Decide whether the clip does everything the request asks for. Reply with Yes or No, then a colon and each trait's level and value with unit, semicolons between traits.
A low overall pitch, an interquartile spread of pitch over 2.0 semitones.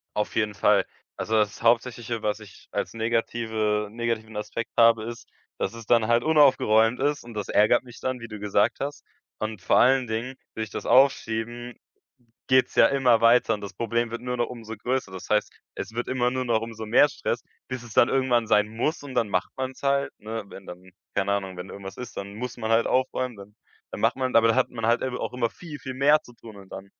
Yes: low, 115 Hz; narrow, 2.6 semitones